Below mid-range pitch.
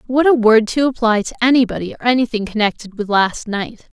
No: high, 230 Hz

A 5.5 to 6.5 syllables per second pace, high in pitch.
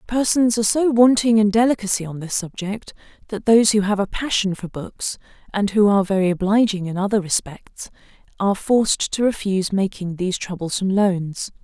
Yes: 5.6 syllables/s; high, 205 Hz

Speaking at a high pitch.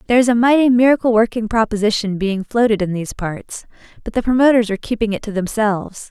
Yes: high, 220 Hz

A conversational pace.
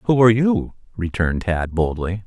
Yes: average, 160 wpm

